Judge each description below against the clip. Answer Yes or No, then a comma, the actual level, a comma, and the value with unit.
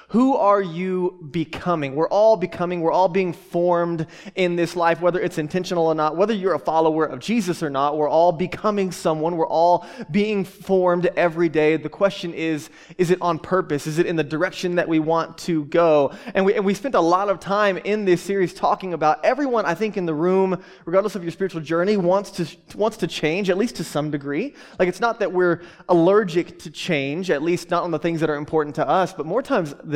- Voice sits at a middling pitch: Yes, medium, 175 Hz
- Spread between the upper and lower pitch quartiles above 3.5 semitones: No, average, 2.8 semitones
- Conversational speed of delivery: No, fast, 225 wpm